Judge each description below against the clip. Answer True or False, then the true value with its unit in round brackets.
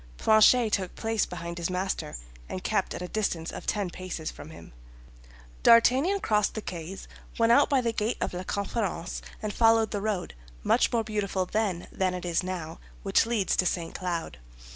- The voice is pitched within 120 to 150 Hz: False (195 Hz)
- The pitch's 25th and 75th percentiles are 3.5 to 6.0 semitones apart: True (3.9 semitones)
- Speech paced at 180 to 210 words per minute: True (185 wpm)